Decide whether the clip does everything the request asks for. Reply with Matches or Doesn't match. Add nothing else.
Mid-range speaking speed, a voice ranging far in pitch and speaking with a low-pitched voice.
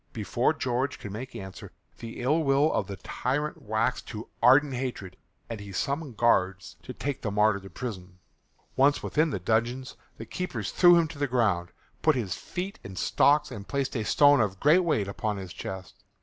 Matches